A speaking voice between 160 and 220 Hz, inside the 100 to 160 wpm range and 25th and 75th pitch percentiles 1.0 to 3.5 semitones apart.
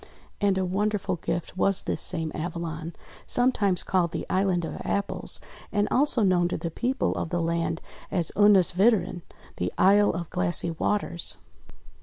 Yes: medium, 185 Hz; average, 155 wpm; average, 3.2 semitones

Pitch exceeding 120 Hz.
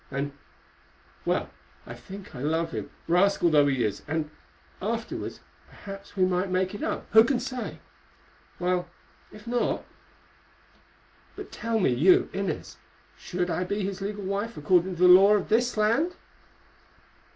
Yes: medium, 185 Hz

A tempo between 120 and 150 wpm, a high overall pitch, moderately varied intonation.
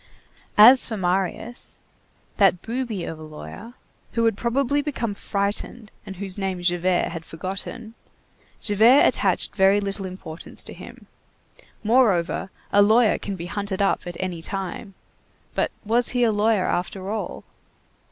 Yes: average, 140 wpm; high, 200 Hz; average, 3.5 semitones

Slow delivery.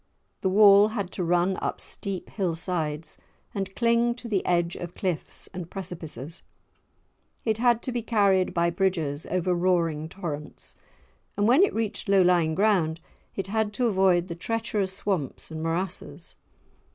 No: average, 155 wpm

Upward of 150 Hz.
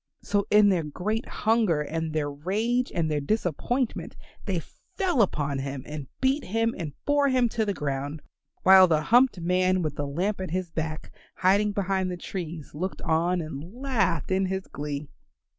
Yes: medium, 185 Hz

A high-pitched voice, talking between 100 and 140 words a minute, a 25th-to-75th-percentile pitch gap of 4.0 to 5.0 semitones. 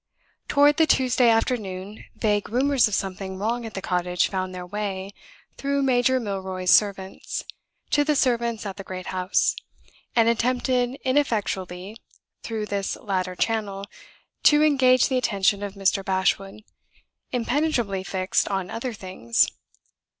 Yes: high, 210 Hz; slow, 135 wpm; average, 4.6 semitones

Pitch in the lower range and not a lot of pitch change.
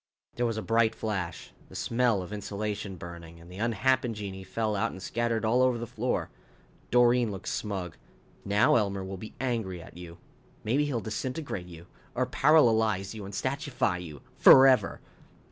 No: low, 110 Hz; average, 4.1 semitones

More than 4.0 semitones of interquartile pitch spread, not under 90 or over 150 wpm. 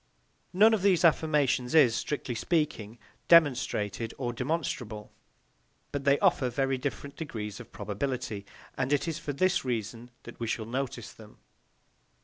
Yes: average, 4.6 semitones; average, 140 wpm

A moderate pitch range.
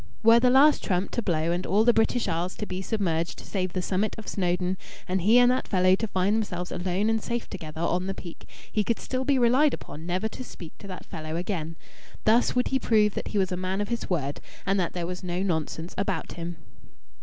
Yes: average, 4.0 semitones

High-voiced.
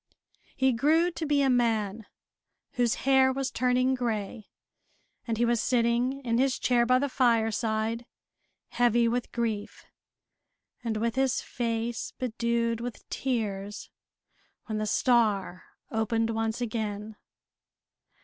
Yes: high, 235 Hz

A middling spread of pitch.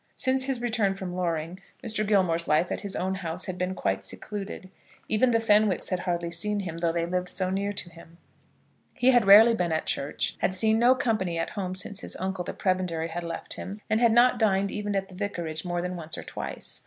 Yes: average, 3.5 semitones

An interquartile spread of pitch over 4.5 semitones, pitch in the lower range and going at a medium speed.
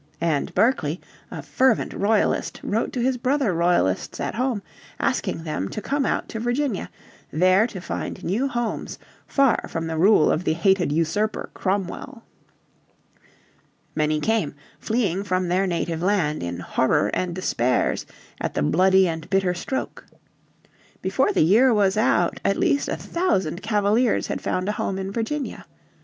No: wide, 5.4 semitones; high, 195 Hz; average, 150 wpm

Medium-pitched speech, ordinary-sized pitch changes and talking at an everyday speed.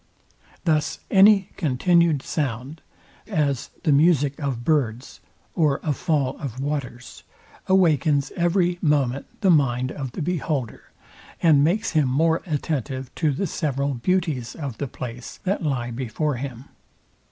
No: medium, 145 Hz; average, 3.9 semitones; slow, 130 wpm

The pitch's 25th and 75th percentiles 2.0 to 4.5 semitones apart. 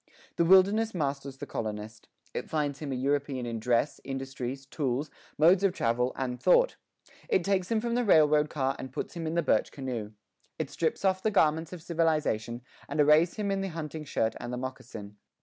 No: average, 5.3 semitones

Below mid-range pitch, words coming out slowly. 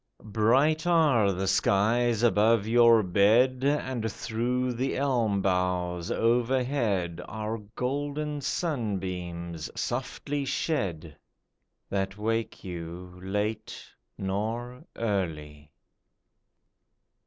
Yes: low, 110 Hz; slow, 85 wpm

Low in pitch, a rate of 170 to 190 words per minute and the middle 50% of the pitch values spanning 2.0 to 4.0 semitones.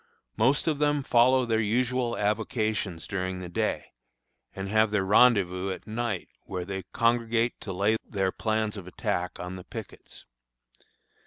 No: low, 110 Hz; average, 150 wpm; average, 3.7 semitones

